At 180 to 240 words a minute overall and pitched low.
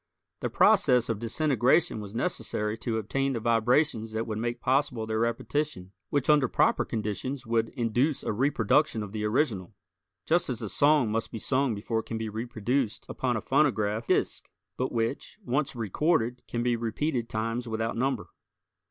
No: average, 170 wpm; low, 115 Hz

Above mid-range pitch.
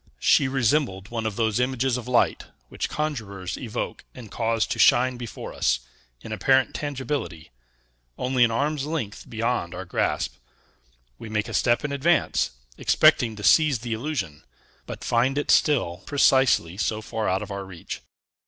No: low, 120 Hz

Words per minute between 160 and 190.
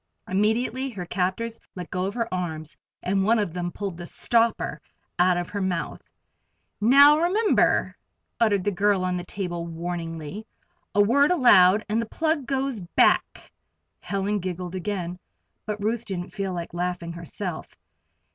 No: average, 150 wpm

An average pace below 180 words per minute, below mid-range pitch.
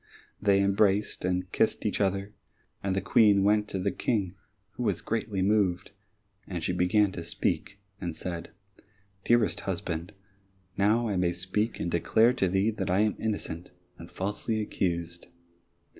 Yes: average, 155 wpm; low, 100 Hz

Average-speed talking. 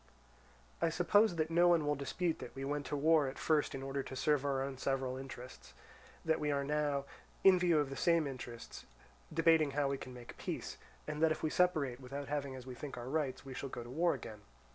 No: fast, 230 wpm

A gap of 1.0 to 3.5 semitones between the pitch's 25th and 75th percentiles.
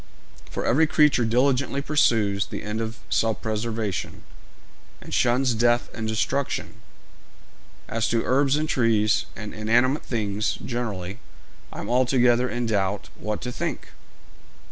Yes: average, 2.9 semitones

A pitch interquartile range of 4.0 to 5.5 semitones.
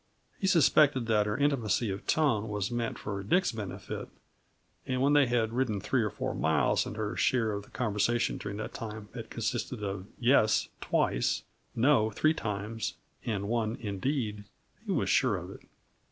No: average, 3.3 semitones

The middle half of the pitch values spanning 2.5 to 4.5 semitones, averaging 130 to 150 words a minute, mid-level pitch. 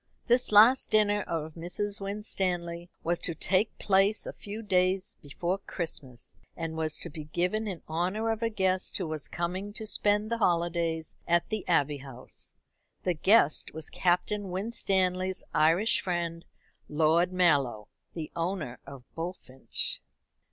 Yes: average, 3.9 semitones; average, 145 wpm; medium, 180 Hz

